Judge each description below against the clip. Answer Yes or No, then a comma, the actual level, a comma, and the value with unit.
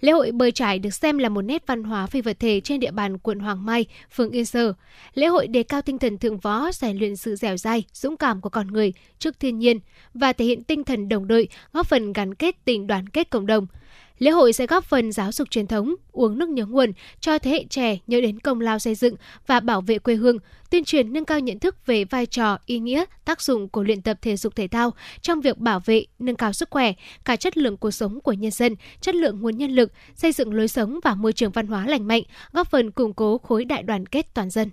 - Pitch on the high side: Yes, high, 235 Hz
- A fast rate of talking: Yes, fast, 260 wpm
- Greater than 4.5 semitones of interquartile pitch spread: No, average, 3.9 semitones